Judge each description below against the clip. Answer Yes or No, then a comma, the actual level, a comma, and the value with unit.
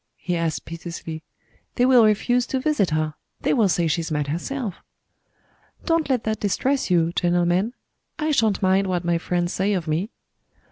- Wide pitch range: Yes, wide, 6.0 semitones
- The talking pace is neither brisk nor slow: Yes, average, 170 wpm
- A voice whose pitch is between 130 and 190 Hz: Yes, medium, 185 Hz